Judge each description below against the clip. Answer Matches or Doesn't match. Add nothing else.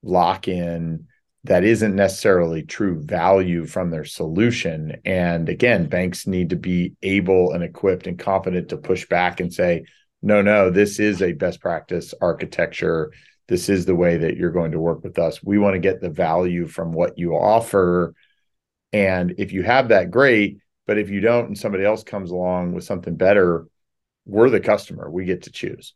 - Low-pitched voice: Matches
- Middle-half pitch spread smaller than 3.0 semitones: Matches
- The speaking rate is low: Doesn't match